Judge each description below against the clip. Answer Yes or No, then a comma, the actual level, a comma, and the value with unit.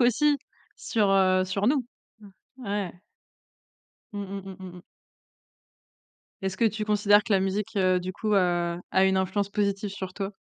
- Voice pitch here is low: No, high, 195 Hz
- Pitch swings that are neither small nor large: No, narrow, 1.8 semitones